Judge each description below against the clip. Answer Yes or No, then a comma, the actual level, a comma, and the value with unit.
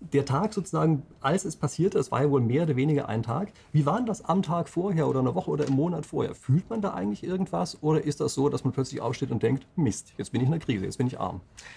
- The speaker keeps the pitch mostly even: No, average, 4.1 semitones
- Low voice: No, medium, 145 Hz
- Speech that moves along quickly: Yes, fast, 275 wpm